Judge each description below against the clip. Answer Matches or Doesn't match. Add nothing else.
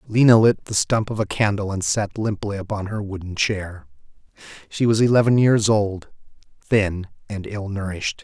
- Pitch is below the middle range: Matches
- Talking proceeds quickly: Doesn't match